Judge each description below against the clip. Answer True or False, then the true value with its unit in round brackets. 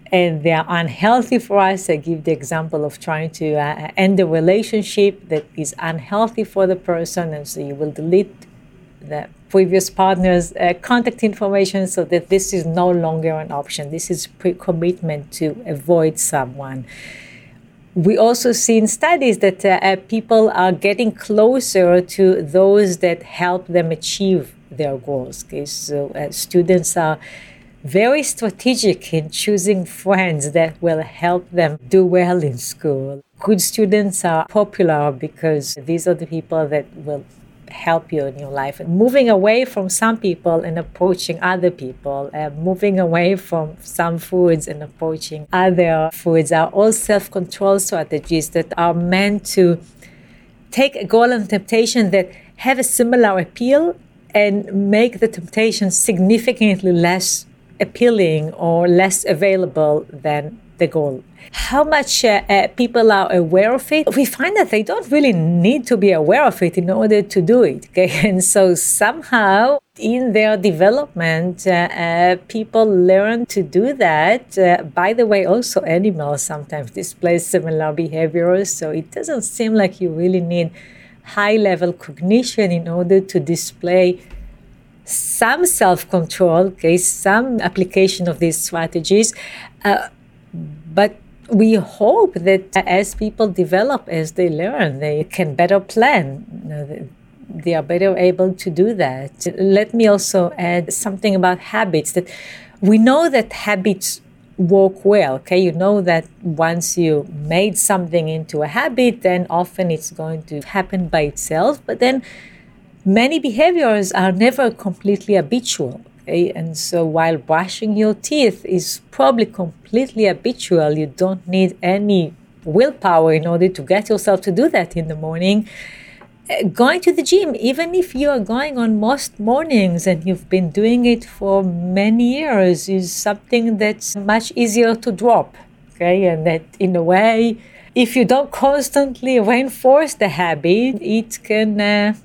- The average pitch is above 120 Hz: True (185 Hz)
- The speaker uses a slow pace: False (150 wpm)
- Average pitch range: True (4.3 semitones)